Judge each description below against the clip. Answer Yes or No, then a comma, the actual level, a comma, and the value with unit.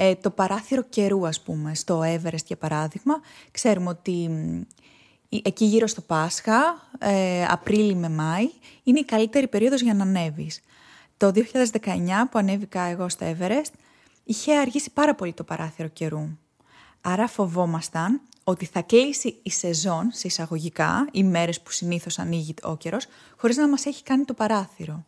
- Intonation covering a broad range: Yes, wide, 5.7 semitones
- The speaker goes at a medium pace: Yes, average, 155 wpm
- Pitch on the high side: Yes, high, 195 Hz